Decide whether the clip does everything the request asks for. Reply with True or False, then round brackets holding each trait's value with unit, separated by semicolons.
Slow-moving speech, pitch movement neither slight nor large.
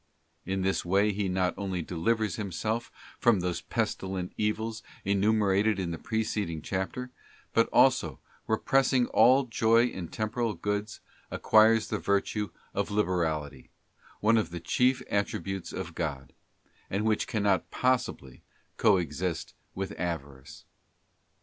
True (125 wpm; 3.7 semitones)